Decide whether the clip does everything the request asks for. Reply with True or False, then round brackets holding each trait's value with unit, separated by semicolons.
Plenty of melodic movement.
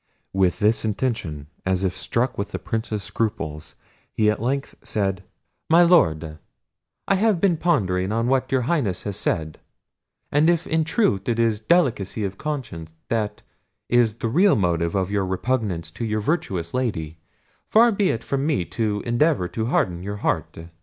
True (6.3 semitones)